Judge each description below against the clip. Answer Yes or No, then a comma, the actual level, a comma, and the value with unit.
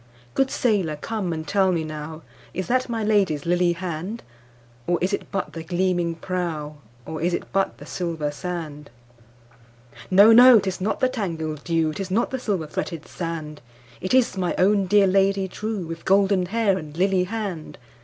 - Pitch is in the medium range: Yes, medium, 175 Hz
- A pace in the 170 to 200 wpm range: No, average, 155 wpm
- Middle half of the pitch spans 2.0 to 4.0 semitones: No, average, 4.4 semitones